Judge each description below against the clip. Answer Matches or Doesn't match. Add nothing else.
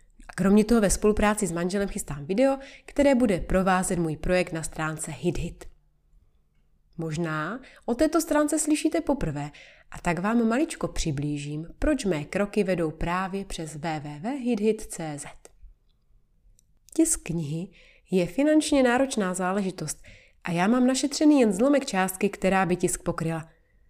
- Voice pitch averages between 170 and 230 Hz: Matches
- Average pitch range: Doesn't match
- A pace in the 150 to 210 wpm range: Doesn't match